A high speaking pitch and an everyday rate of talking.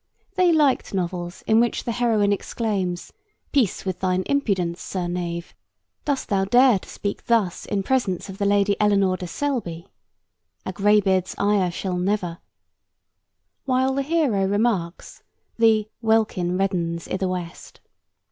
Yes: high, 200 Hz; average, 145 wpm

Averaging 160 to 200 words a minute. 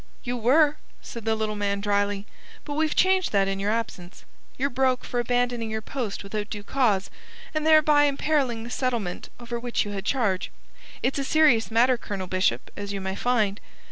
Yes: average, 185 wpm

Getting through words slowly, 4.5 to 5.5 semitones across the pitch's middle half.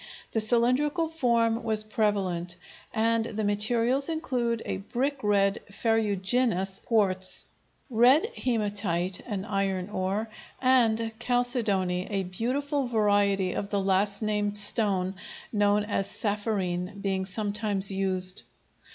No: slow, 110 wpm; average, 3.2 semitones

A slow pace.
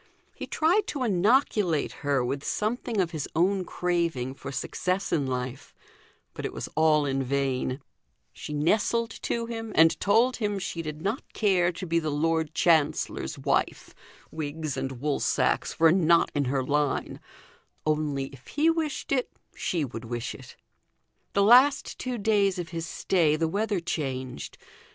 No: average, 160 wpm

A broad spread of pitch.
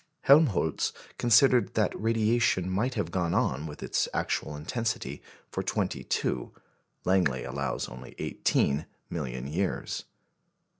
Yes: wide, 8.3 semitones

